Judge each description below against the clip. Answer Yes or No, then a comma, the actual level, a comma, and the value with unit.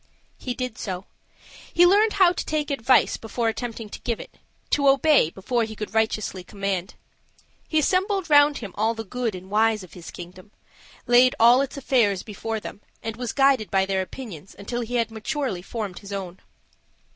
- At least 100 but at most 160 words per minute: No, average, 180 wpm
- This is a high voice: Yes, high, 225 Hz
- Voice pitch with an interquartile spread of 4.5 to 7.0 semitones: Yes, average, 5.1 semitones